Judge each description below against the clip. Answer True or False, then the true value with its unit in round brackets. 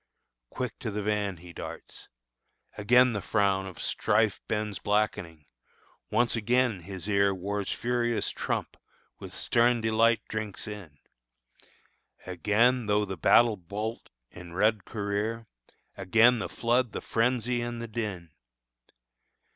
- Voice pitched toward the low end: True (105 Hz)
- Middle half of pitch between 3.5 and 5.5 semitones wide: False (2.9 semitones)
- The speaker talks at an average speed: False (125 wpm)